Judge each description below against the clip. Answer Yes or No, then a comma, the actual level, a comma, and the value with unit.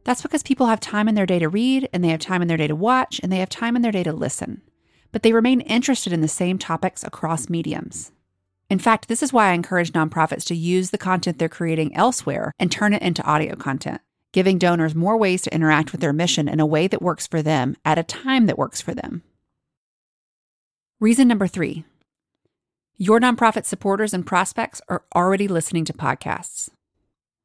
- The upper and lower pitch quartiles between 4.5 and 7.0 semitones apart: Yes, average, 5.2 semitones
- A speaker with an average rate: No, fast, 210 wpm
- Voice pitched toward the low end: No, medium, 185 Hz